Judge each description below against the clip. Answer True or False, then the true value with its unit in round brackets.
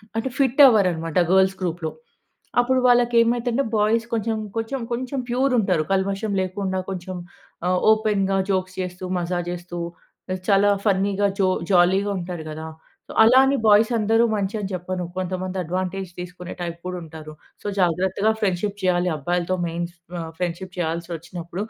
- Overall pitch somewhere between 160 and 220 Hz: True (190 Hz)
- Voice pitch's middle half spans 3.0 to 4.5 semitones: True (3.3 semitones)